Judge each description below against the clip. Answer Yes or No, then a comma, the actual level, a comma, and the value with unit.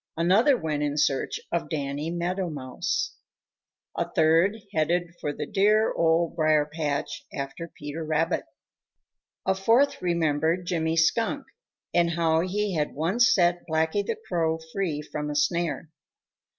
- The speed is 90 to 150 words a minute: Yes, average, 140 wpm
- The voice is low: No, medium, 165 Hz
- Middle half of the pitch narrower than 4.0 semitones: Yes, average, 3.0 semitones